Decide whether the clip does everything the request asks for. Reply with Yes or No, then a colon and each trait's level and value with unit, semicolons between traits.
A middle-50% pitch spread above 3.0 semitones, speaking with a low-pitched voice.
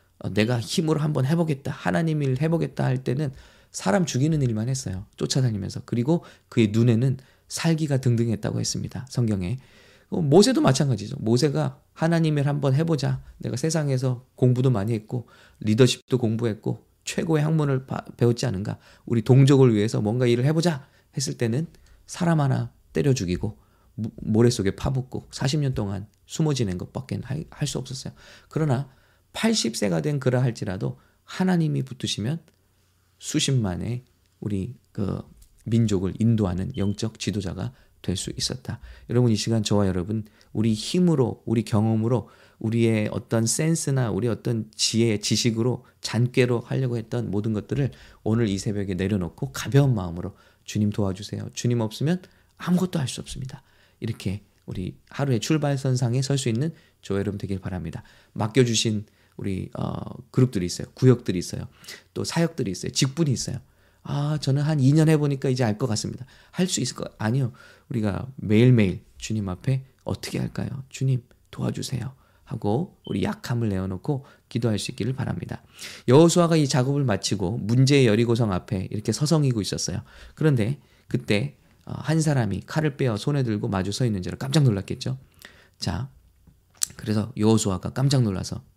Yes: average, 4.9 semitones; low, 120 Hz